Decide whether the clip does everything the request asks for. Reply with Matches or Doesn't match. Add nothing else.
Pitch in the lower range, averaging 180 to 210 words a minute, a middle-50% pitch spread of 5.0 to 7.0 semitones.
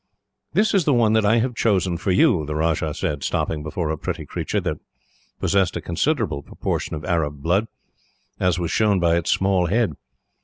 Matches